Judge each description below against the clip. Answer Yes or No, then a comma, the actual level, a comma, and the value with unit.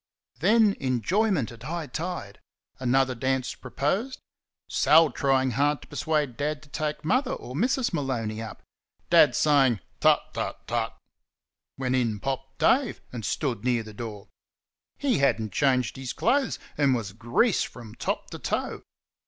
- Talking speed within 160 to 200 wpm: No, average, 150 wpm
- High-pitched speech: No, low, 135 Hz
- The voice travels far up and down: No, average, 4.9 semitones